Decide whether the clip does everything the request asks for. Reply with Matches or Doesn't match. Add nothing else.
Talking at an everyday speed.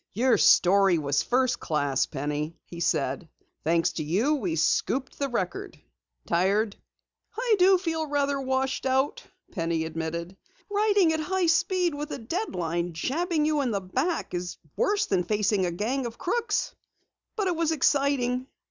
Matches